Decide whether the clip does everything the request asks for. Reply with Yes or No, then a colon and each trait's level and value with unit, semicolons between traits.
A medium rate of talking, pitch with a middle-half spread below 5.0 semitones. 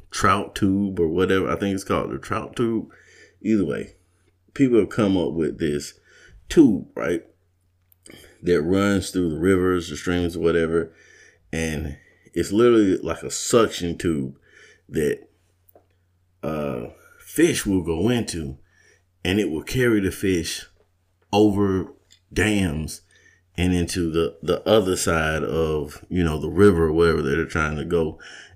Yes: average, 145 wpm; average, 2.7 semitones